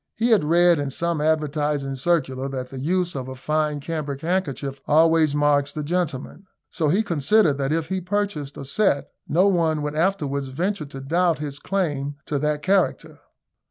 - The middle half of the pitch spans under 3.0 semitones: No, average, 3.6 semitones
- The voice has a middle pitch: Yes, medium, 150 Hz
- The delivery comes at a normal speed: Yes, average, 175 wpm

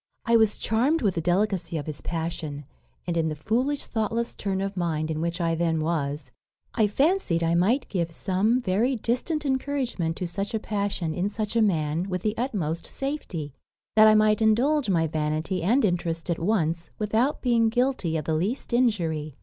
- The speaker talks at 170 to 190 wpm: Yes, average, 185 wpm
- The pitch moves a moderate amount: No, wide, 5.8 semitones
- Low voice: No, high, 190 Hz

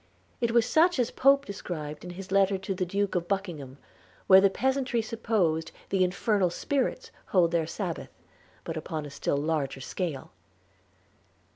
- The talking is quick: No, average, 155 wpm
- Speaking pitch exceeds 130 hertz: Yes, high, 190 Hz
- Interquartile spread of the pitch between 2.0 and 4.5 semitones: No, wide, 5.4 semitones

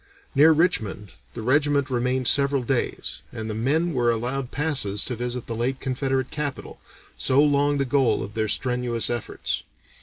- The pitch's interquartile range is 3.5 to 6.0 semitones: No, average, 3.1 semitones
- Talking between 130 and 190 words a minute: Yes, average, 160 wpm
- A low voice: Yes, low, 130 Hz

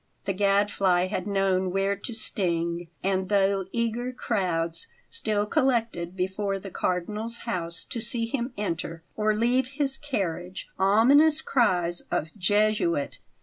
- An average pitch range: Yes, average, 4.2 semitones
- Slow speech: Yes, slow, 130 wpm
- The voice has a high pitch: Yes, high, 200 Hz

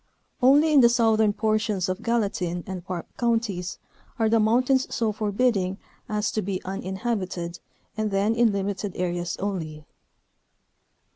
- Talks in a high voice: Yes, high, 205 Hz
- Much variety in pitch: No, average, 3.6 semitones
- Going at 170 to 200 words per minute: No, average, 140 wpm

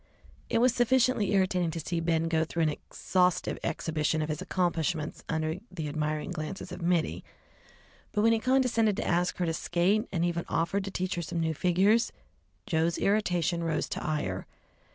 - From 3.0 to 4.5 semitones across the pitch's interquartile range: Yes, average, 3.5 semitones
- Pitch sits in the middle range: Yes, medium, 175 Hz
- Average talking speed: Yes, average, 175 wpm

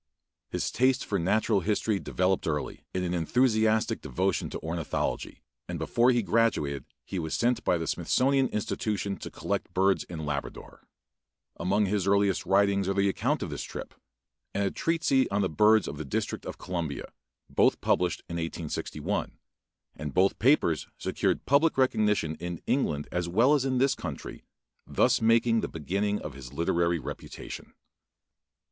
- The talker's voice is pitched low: Yes, low, 100 Hz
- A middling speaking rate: Yes, average, 160 wpm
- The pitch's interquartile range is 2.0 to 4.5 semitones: No, average, 5.1 semitones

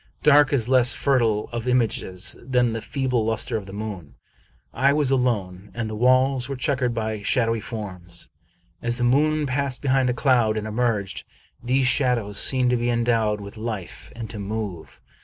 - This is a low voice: Yes, low, 120 Hz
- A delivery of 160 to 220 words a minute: Yes, average, 175 wpm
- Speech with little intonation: No, average, 3.1 semitones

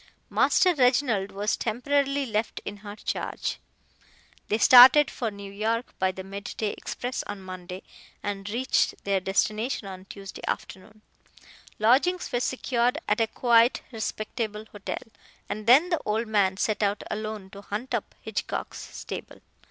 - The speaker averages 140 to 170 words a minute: Yes, average, 145 wpm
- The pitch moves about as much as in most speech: Yes, average, 3.5 semitones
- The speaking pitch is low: No, high, 215 Hz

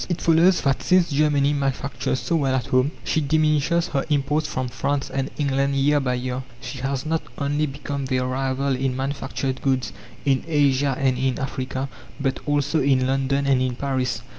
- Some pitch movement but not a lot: No, narrow, 1.9 semitones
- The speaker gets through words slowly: No, average, 180 wpm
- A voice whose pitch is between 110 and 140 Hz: Yes, low, 135 Hz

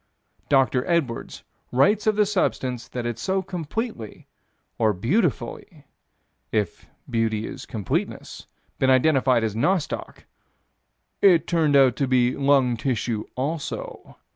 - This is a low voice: Yes, low, 130 Hz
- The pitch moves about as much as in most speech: No, wide, 6.1 semitones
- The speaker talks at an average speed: No, slow, 115 wpm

